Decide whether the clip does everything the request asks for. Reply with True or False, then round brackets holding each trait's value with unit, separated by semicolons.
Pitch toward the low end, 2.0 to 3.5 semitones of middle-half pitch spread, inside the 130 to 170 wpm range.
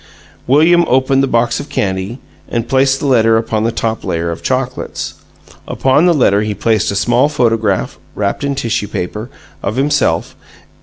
False (120 Hz; 4.0 semitones; 165 wpm)